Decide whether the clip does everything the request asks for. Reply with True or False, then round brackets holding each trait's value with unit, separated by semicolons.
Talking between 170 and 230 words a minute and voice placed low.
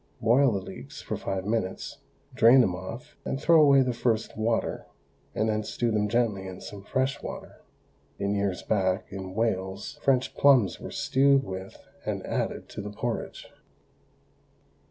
False (155 wpm; 110 Hz)